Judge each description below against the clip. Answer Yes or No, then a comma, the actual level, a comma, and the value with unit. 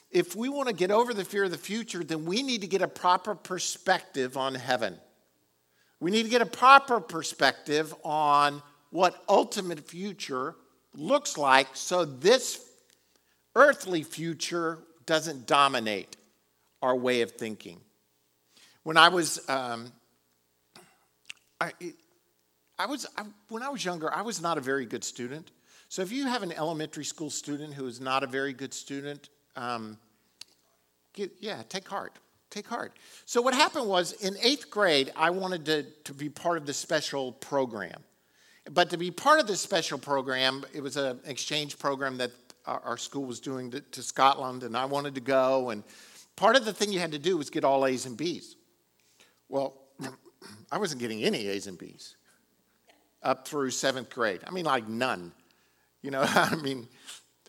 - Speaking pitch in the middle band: Yes, medium, 145 Hz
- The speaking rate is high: No, average, 170 wpm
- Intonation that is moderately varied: No, wide, 6.0 semitones